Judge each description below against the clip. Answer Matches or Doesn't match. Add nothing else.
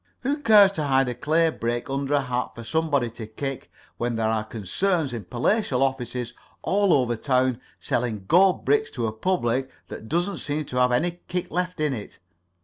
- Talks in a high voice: Doesn't match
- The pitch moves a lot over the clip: Matches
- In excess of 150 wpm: Matches